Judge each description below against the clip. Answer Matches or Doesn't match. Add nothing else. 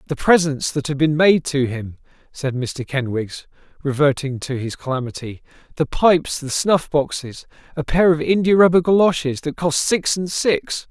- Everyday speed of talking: Matches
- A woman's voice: Doesn't match